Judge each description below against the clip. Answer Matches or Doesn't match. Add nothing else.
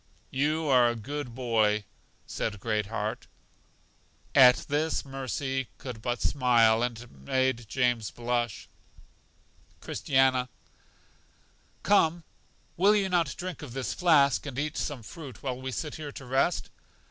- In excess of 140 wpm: Doesn't match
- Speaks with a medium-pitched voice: Doesn't match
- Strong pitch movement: Doesn't match